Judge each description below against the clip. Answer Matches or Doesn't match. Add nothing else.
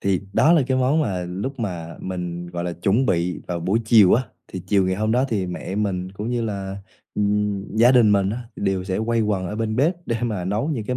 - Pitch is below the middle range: Matches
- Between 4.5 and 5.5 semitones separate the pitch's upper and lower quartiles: Doesn't match